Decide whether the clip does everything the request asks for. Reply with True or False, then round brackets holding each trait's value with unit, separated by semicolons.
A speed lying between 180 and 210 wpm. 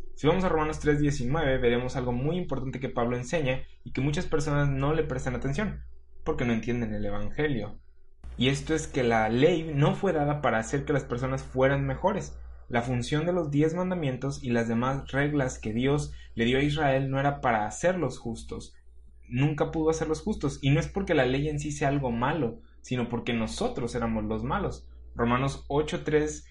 True (190 wpm)